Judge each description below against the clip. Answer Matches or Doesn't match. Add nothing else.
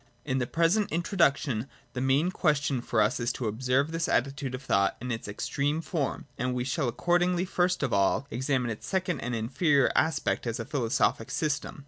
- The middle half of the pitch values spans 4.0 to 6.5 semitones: Matches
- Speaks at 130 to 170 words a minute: Doesn't match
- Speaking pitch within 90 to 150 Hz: Matches